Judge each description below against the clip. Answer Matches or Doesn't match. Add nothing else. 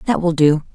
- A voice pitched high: Doesn't match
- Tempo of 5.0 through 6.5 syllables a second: Doesn't match